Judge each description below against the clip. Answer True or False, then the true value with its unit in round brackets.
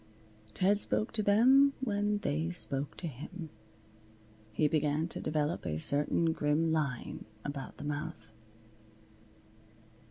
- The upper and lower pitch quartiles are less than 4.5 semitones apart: False (5.4 semitones)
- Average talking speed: False (120 wpm)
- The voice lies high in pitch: False (160 Hz)